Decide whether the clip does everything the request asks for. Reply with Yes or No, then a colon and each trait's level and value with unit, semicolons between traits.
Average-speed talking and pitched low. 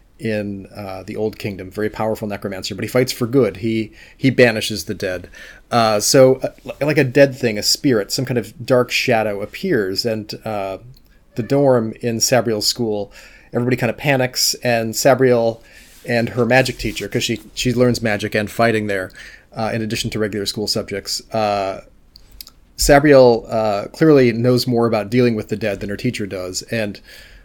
Yes: average, 175 wpm; low, 115 Hz